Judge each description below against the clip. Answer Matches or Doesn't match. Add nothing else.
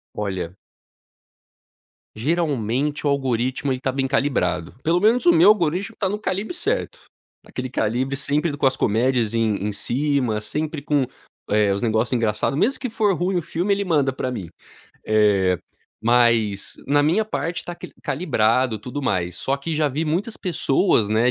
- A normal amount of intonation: Doesn't match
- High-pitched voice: Doesn't match